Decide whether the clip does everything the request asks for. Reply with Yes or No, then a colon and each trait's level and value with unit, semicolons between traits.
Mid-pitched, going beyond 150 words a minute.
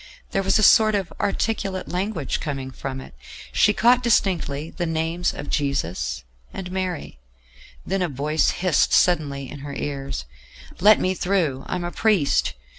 Yes: medium, 170 Hz; average, 160 wpm